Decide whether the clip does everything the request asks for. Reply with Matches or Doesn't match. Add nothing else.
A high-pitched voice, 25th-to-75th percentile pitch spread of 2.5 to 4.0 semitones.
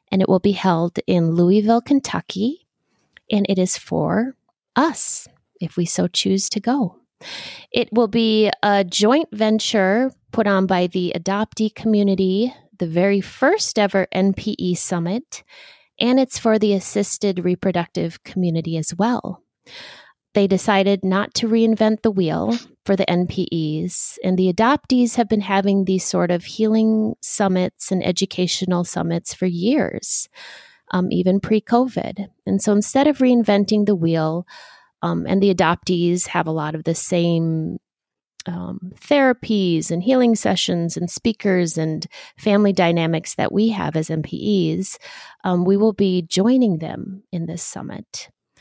Matches